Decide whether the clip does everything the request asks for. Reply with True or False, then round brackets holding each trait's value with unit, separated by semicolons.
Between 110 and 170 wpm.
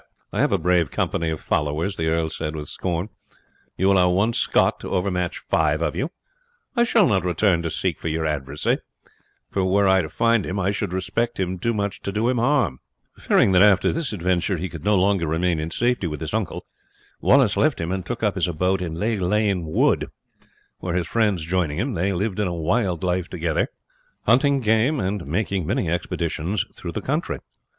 False (200 wpm)